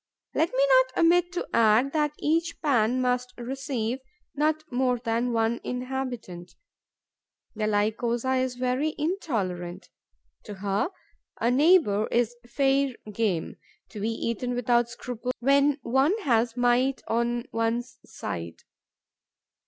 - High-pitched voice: Yes, high, 245 Hz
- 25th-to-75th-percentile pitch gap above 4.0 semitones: No, average, 3.1 semitones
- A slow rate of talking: Yes, slow, 120 wpm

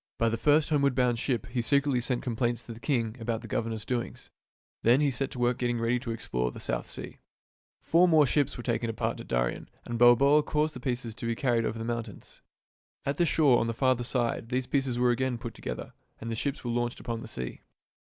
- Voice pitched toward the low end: Yes, low, 120 Hz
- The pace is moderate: No, fast, 230 wpm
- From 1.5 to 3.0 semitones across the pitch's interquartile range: Yes, narrow, 2.6 semitones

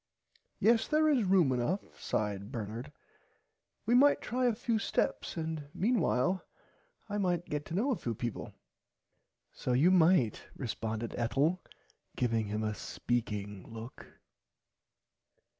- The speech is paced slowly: Yes, slow, 125 wpm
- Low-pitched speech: No, medium, 145 Hz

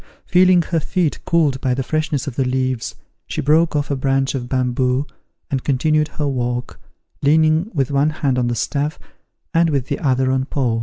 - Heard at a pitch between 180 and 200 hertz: No, medium, 140 Hz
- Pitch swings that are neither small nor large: Yes, average, 3.2 semitones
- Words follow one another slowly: No, average, 190 wpm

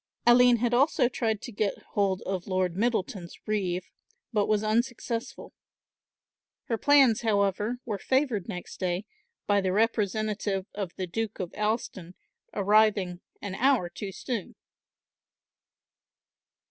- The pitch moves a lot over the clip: No, average, 3.4 semitones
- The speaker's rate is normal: No, slow, 120 wpm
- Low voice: No, high, 210 Hz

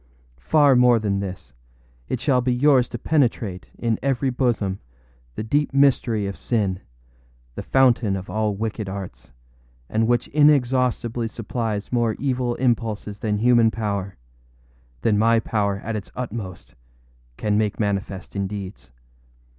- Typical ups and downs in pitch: Yes, average, 3.8 semitones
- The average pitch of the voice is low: Yes, low, 110 Hz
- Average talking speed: No, slow, 130 wpm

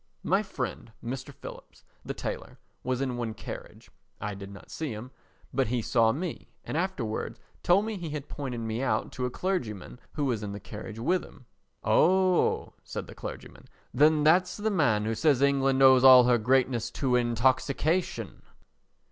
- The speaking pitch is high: No, low, 130 Hz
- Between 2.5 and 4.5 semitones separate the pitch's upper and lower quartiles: No, average, 5.1 semitones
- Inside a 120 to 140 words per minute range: No, average, 175 wpm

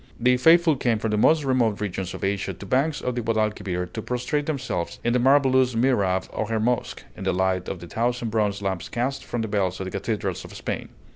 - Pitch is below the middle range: Yes, low, 110 Hz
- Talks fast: Yes, fast, 225 wpm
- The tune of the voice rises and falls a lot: No, average, 4.4 semitones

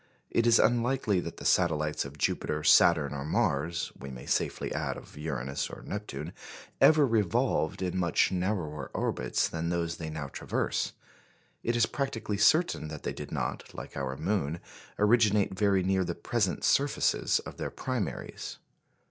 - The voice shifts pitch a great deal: Yes, wide, 6.0 semitones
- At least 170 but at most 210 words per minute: No, average, 155 wpm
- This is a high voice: No, very low, 90 Hz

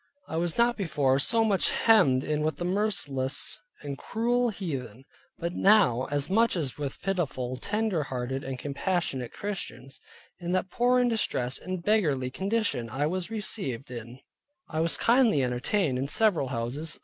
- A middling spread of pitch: No, wide, 7.6 semitones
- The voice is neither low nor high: Yes, medium, 165 Hz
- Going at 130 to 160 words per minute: Yes, average, 155 wpm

